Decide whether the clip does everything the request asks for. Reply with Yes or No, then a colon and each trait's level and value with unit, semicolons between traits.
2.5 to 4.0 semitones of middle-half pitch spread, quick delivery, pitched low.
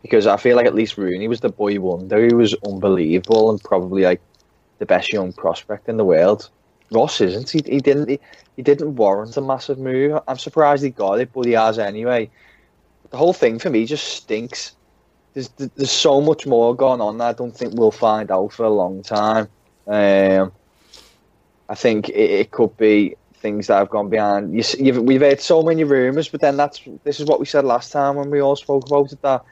No: average, 5.2 semitones; fast, 220 wpm; low, 120 Hz